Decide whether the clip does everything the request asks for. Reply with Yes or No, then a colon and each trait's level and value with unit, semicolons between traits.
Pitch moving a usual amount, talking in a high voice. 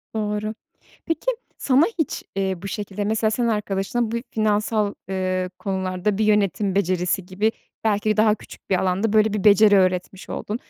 No: narrow, 2.2 semitones; high, 205 Hz